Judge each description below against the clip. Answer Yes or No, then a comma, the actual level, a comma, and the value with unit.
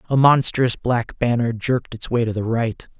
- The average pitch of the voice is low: Yes, low, 120 Hz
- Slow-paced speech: No, average, 200 wpm